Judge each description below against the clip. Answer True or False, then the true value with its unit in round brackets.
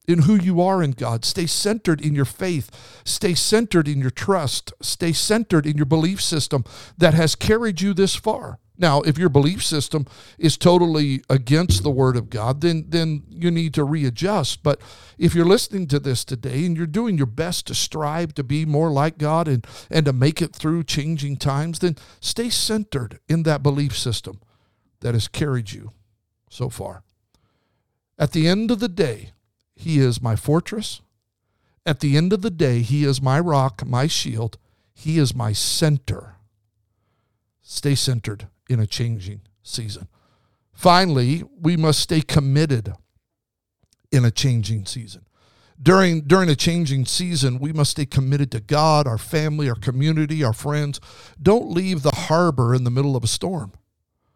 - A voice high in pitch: False (140 Hz)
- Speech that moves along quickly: False (170 wpm)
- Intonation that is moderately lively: False (6.0 semitones)